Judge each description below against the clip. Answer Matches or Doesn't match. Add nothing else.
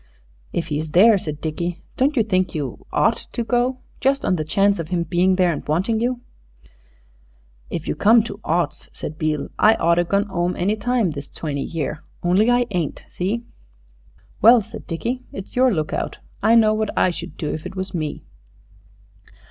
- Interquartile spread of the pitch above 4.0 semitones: Matches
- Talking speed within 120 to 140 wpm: Doesn't match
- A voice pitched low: Doesn't match